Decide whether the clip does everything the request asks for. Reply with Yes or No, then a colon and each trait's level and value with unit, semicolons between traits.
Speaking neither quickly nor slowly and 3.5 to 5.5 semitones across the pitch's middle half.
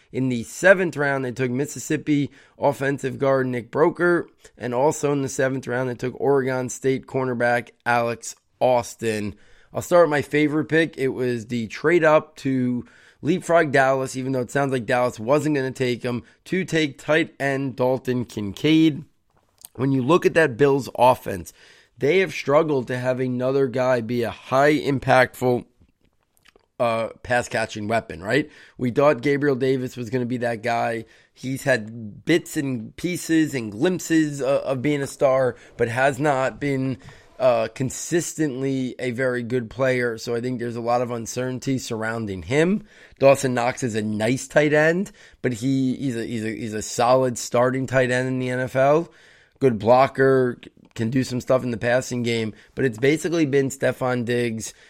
No: average, 175 wpm; average, 2.7 semitones